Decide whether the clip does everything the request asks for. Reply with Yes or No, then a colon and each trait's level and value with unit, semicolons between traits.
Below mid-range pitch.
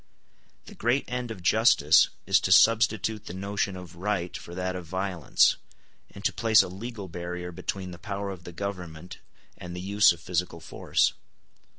Yes: very low, 95 Hz